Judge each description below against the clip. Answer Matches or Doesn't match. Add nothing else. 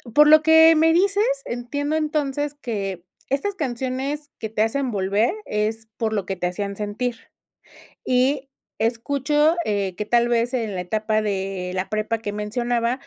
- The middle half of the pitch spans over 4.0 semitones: Matches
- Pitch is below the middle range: Doesn't match